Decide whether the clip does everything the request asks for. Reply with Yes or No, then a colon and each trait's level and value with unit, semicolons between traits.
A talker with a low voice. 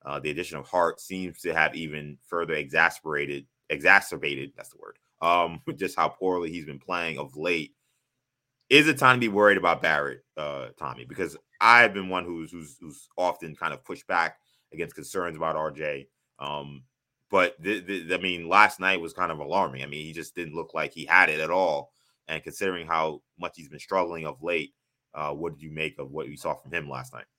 Yes: very low, 85 Hz